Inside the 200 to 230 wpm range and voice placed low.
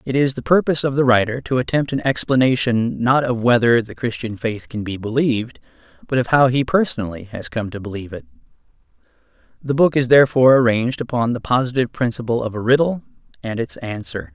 No: average, 190 wpm; low, 125 Hz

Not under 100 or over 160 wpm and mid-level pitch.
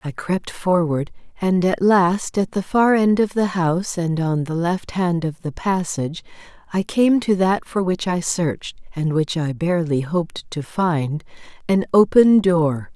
No: average, 175 wpm; medium, 175 Hz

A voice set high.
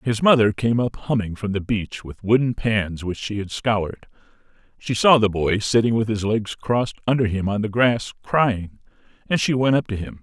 No: low, 110 Hz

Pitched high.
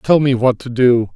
No: low, 125 Hz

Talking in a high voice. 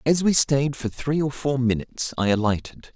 No: low, 135 Hz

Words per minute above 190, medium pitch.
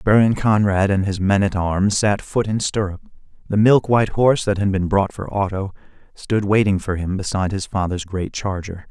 No: average, 200 wpm; low, 100 Hz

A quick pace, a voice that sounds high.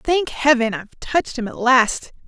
No: average, 185 wpm; very high, 255 Hz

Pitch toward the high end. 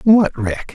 No: medium, 165 Hz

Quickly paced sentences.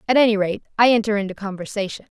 No: average, 190 wpm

